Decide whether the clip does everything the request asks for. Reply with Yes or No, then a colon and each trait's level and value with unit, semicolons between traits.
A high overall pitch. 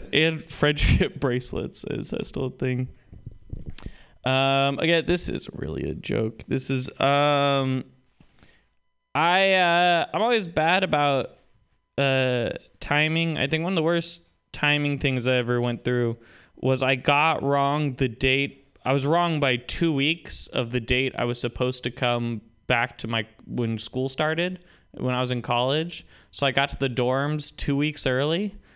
No: low, 135 Hz